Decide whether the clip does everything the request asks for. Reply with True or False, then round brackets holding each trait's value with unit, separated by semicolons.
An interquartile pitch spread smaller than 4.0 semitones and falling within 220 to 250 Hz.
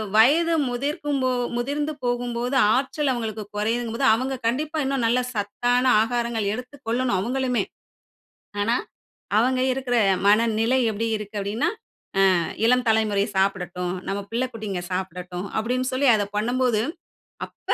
True (3.3 semitones; 235 Hz)